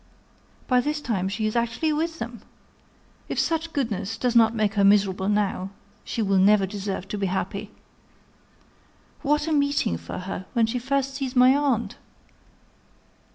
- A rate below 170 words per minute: Yes, average, 155 wpm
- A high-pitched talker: Yes, high, 225 Hz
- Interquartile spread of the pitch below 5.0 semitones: No, wide, 5.6 semitones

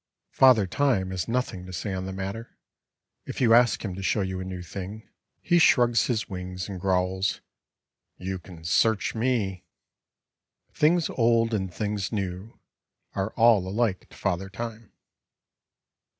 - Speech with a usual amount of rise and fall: Yes, average, 3.7 semitones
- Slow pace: No, average, 150 wpm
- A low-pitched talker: Yes, low, 100 Hz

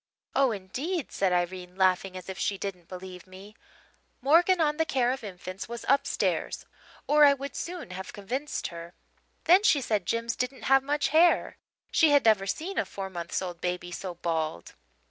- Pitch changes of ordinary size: No, wide, 7.4 semitones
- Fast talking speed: No, average, 180 wpm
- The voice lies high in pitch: Yes, high, 205 Hz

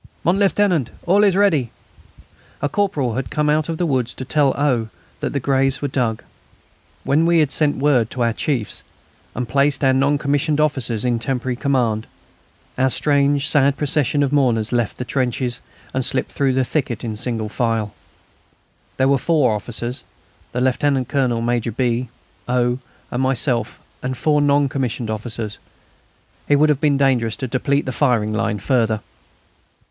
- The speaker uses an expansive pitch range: No, average, 3.3 semitones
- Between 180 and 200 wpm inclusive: No, average, 165 wpm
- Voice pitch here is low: Yes, low, 130 Hz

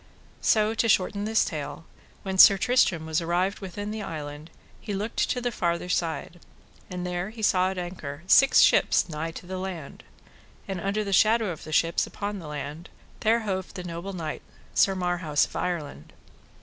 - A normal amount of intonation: Yes, average, 3.5 semitones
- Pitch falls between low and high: Yes, medium, 180 Hz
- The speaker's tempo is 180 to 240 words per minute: Yes, average, 185 wpm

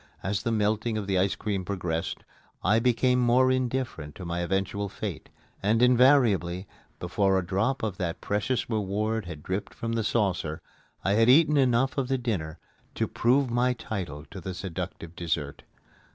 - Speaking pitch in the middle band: No, low, 105 Hz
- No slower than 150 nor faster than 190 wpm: Yes, average, 165 wpm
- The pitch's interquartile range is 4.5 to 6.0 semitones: Yes, average, 4.9 semitones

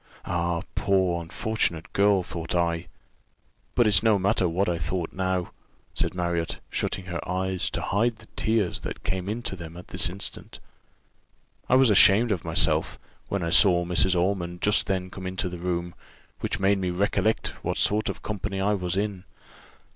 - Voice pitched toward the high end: No, very low, 95 Hz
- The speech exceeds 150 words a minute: Yes, average, 170 wpm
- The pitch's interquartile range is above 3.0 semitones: No, narrow, 2.5 semitones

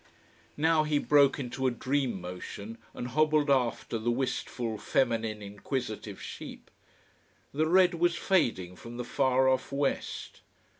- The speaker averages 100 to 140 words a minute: Yes, slow, 135 wpm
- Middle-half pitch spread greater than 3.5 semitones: Yes, average, 4.2 semitones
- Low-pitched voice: Yes, low, 130 Hz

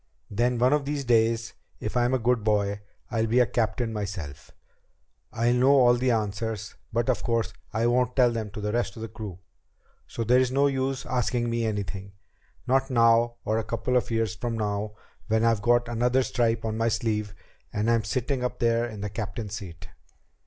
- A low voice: Yes, low, 115 Hz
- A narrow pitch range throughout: Yes, narrow, 2.3 semitones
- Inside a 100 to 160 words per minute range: No, average, 195 wpm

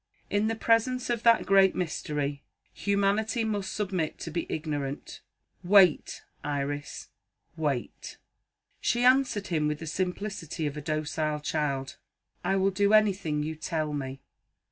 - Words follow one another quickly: No, slow, 135 wpm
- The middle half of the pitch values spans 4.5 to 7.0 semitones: Yes, wide, 5.4 semitones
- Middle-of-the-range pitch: Yes, medium, 170 Hz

